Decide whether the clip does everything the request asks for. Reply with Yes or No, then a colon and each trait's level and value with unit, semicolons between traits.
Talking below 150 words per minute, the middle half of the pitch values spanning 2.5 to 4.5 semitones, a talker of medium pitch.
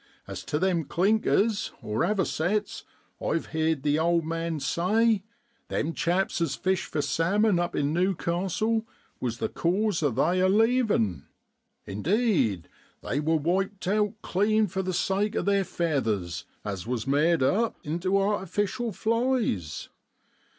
No: slow, 135 wpm; wide, 5.4 semitones; medium, 175 Hz